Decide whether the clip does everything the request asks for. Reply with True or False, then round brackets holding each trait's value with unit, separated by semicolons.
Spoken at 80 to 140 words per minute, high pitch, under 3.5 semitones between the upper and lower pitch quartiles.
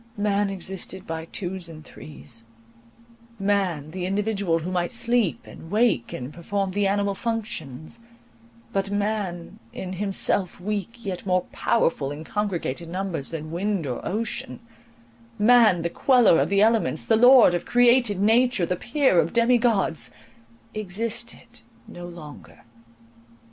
False (135 wpm; 195 Hz; 4.2 semitones)